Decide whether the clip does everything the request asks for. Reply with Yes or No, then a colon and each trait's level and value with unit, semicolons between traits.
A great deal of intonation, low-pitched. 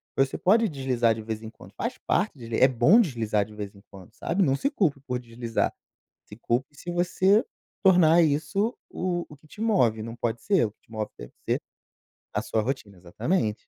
Yes: wide, 7.8 semitones; low, 130 Hz